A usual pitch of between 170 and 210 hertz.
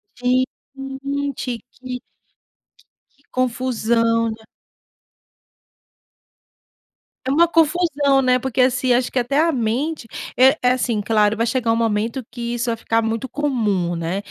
No: very high, 250 Hz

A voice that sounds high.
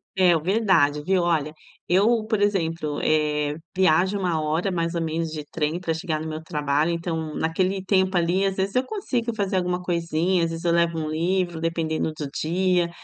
No: medium, 170 Hz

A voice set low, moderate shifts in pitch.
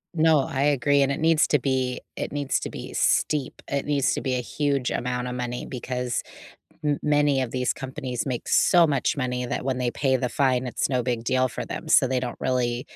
No: low, 130 Hz; narrow, 2.3 semitones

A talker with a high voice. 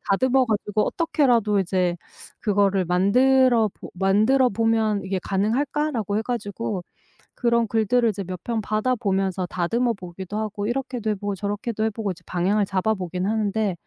Yes: high, 210 Hz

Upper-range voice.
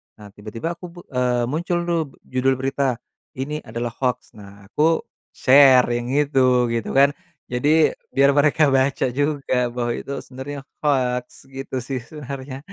No: low, 135 Hz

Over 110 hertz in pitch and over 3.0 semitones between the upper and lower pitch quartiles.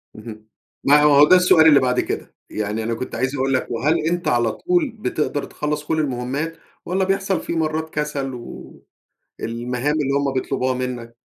Yes: medium, 140 Hz; average, 4.2 semitones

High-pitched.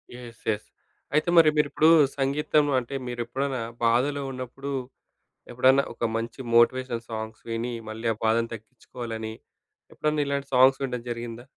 No: low, 125 Hz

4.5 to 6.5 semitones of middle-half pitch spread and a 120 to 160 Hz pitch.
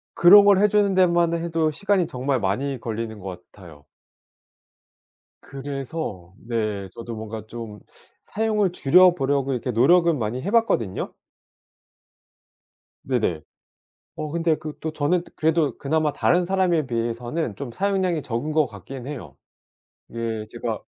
No: wide, 6.9 semitones; medium, 140 Hz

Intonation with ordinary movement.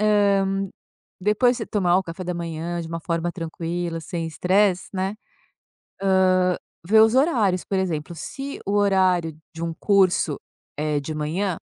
Yes: average, 3.3 semitones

